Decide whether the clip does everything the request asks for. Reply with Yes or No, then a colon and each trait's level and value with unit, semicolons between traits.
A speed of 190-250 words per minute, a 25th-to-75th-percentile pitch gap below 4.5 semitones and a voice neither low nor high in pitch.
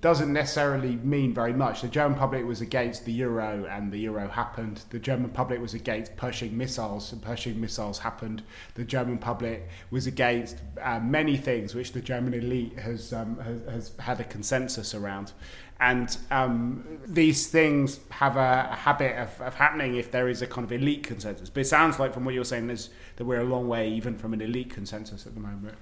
No: fast, 205 wpm; narrow, 2.5 semitones; low, 120 Hz